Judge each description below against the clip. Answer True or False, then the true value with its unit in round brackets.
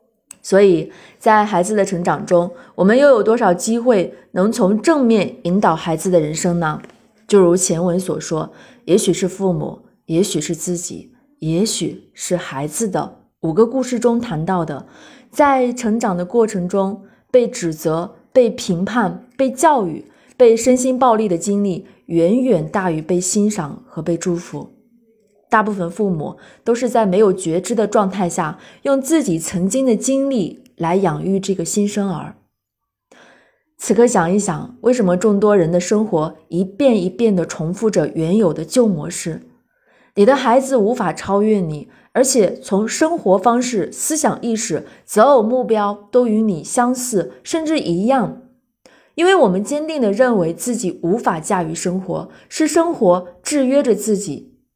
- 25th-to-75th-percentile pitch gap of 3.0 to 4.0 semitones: False (5.3 semitones)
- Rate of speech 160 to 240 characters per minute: True (230 characters per minute)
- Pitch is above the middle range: True (205 Hz)